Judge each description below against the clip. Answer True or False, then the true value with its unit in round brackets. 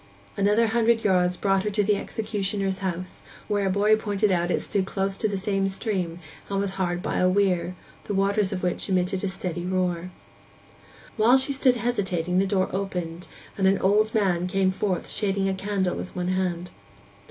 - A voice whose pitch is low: False (195 Hz)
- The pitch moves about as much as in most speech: False (2.0 semitones)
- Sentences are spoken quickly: False (185 wpm)